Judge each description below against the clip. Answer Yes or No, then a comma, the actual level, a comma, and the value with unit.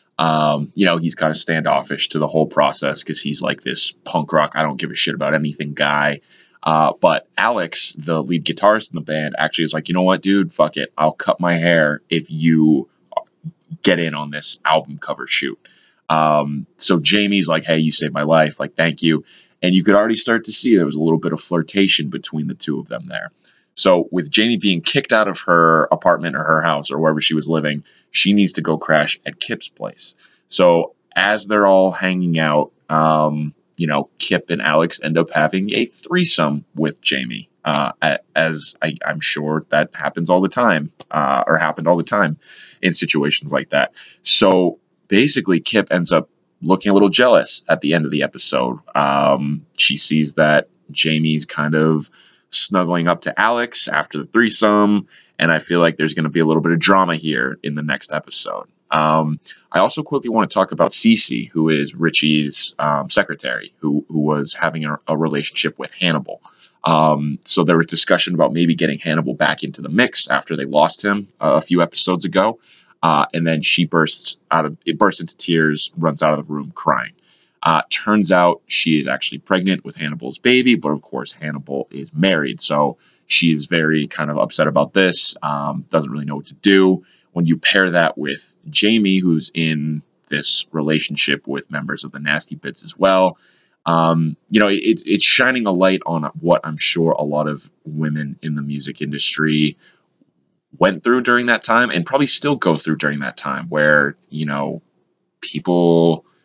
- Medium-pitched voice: No, very low, 80 Hz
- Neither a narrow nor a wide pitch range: Yes, average, 3.6 semitones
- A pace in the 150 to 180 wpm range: No, average, 195 wpm